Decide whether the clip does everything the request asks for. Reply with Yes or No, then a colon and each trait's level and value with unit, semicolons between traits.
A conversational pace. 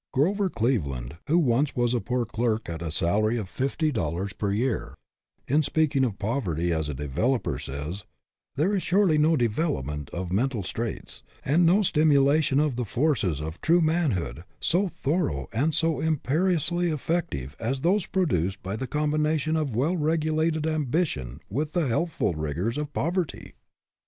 Yes: average, 160 wpm